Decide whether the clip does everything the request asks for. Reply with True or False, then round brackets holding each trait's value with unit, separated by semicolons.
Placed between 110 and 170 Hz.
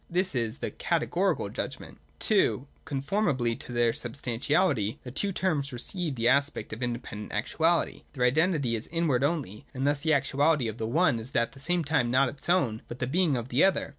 True (135 Hz)